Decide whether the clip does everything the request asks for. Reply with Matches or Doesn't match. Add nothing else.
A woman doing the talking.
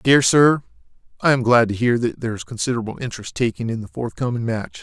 Doesn't match